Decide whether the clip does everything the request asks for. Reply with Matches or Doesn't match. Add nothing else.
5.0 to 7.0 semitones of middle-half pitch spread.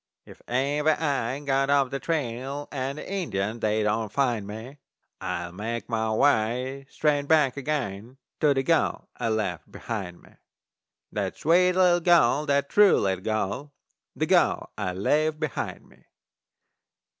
Matches